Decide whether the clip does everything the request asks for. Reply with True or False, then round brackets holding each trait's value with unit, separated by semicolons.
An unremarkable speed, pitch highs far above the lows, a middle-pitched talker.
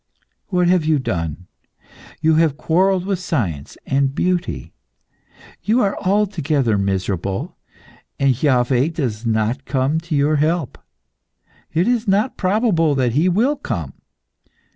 False (125 wpm; 6.4 semitones; 155 Hz)